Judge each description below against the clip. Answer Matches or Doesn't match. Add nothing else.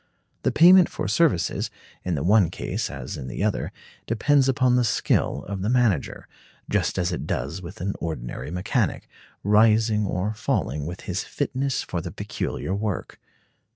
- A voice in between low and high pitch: Doesn't match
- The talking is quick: Doesn't match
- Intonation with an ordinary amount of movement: Doesn't match